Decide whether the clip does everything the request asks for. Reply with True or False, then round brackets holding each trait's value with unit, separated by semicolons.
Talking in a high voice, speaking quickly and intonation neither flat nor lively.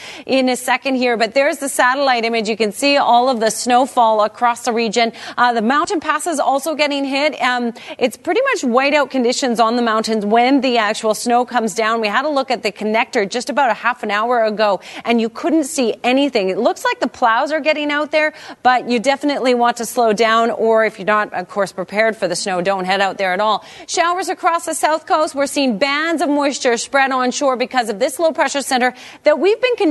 True (250 Hz; 230 wpm; 4.3 semitones)